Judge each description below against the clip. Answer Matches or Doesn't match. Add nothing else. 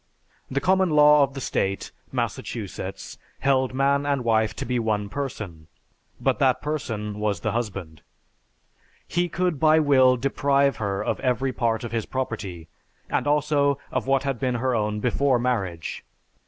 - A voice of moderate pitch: Doesn't match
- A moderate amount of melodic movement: Matches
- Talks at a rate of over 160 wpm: Doesn't match